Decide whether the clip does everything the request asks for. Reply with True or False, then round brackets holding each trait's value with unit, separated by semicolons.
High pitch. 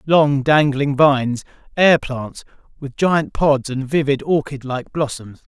False (140 Hz)